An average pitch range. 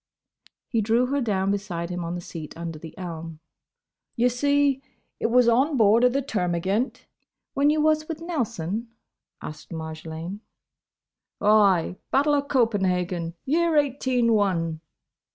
No: wide, 7.5 semitones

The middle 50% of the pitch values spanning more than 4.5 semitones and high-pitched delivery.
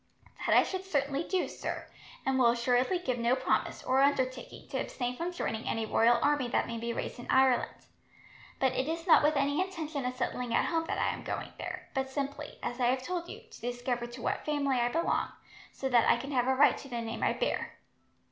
No: average, 3.3 semitones; very high, 260 Hz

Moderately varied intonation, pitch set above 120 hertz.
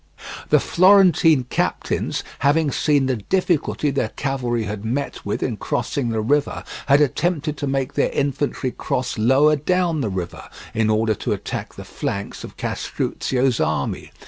Yes: average, 4.2 semitones; low, 135 Hz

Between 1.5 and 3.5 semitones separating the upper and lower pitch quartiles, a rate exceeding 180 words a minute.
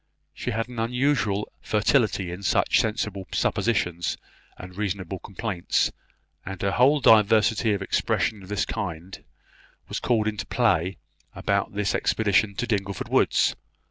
No: average, 2.7 semitones; slow, 135 wpm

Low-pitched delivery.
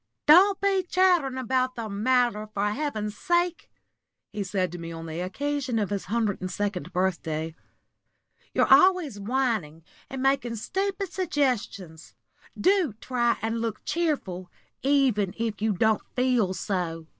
No: high, 230 Hz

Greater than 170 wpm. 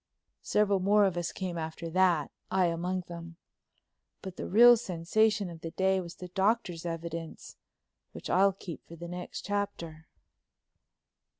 No: average, 145 wpm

